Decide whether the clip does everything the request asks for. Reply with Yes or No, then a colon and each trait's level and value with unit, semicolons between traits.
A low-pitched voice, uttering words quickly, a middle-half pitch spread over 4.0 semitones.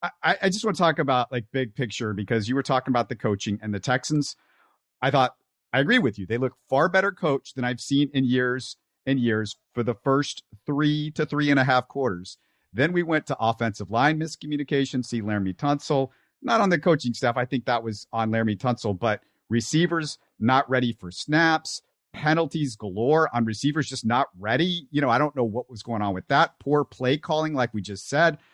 Yes: low, 130 Hz; fast, 210 wpm; average, 4.4 semitones